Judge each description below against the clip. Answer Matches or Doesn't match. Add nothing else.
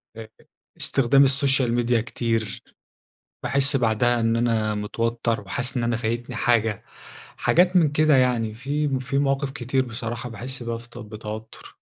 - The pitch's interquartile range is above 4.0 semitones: Doesn't match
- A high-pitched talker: Doesn't match